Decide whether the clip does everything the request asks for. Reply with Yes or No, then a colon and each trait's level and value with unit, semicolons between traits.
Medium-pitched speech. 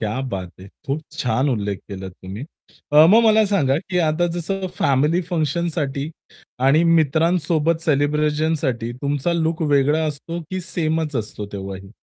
Yes: medium, 150 Hz